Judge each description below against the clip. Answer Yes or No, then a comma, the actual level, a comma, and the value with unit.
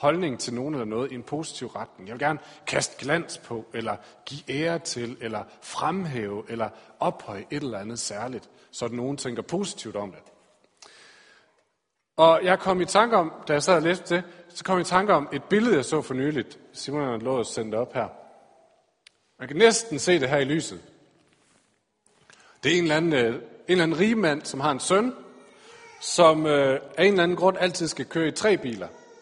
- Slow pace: No, average, 200 wpm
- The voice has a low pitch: No, medium, 150 Hz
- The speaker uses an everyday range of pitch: No, wide, 6.3 semitones